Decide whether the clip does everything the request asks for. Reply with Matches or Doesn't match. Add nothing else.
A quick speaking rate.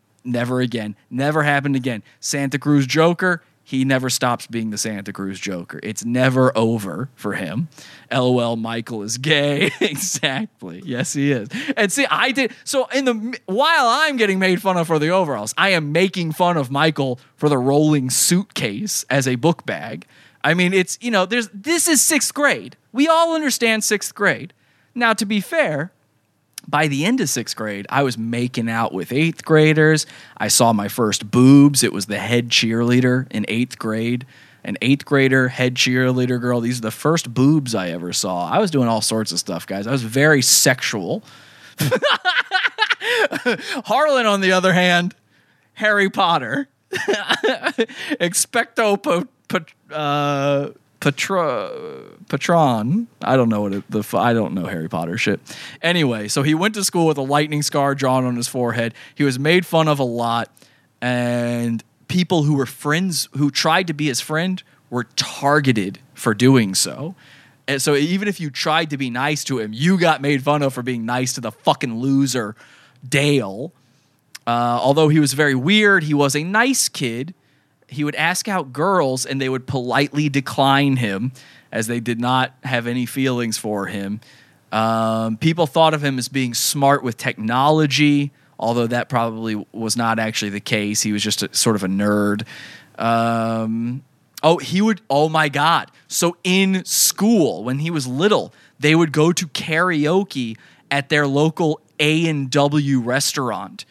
Doesn't match